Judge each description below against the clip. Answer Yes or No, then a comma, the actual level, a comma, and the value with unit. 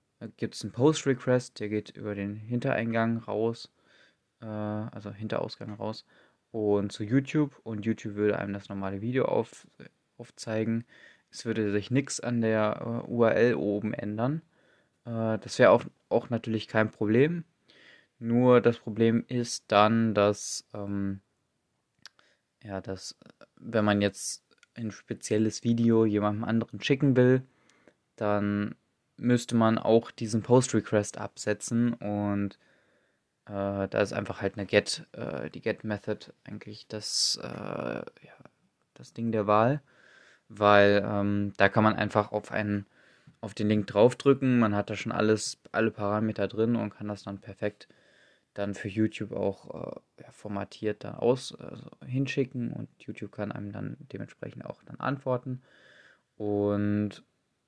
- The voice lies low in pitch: Yes, low, 110 Hz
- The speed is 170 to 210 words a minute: No, average, 140 wpm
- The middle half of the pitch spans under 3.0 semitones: Yes, narrow, 2.4 semitones